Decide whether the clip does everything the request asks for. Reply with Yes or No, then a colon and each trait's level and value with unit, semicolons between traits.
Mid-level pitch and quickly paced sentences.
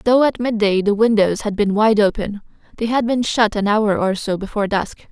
No: high, 215 Hz; fast, 225 wpm